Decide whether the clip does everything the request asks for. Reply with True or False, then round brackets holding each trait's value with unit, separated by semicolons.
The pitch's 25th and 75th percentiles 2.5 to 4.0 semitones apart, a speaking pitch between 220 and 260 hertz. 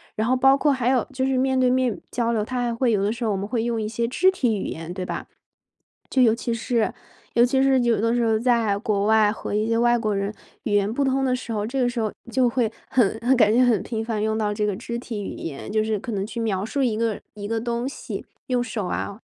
True (2.8 semitones; 230 Hz)